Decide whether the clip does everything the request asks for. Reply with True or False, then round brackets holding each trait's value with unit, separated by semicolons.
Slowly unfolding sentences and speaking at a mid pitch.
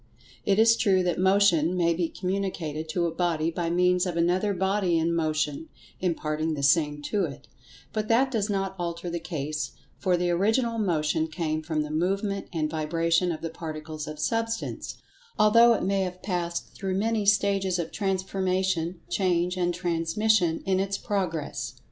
False (165 wpm; 175 Hz)